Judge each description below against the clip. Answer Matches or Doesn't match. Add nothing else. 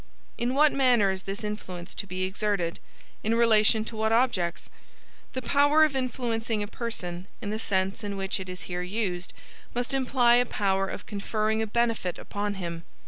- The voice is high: Matches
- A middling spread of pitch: Matches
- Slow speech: Doesn't match